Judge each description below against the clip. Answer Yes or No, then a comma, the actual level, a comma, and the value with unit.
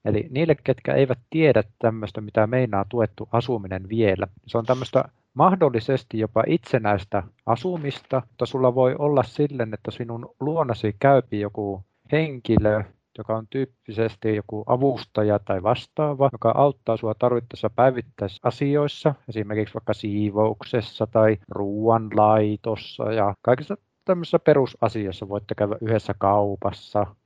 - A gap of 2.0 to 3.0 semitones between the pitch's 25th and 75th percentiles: No, average, 3.6 semitones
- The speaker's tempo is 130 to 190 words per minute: No, average, 120 wpm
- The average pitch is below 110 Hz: No, low, 115 Hz